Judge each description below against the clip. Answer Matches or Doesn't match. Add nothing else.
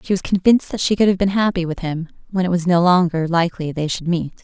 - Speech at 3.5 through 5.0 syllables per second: Doesn't match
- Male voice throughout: Doesn't match